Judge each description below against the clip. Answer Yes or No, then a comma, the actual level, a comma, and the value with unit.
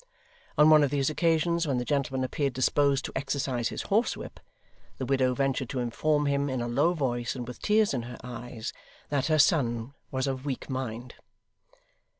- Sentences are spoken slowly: No, average, 180 wpm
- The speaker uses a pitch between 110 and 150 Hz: Yes, low, 135 Hz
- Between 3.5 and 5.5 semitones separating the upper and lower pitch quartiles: No, average, 2.9 semitones